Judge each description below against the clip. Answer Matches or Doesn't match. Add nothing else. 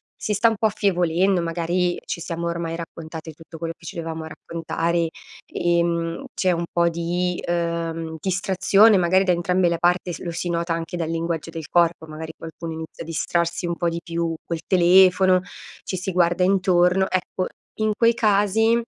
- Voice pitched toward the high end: Doesn't match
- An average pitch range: Doesn't match